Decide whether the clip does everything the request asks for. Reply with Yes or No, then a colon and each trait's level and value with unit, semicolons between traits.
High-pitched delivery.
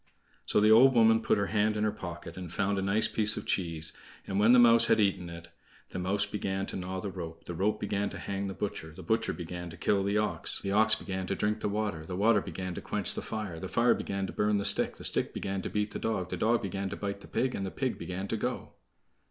No: low, 100 Hz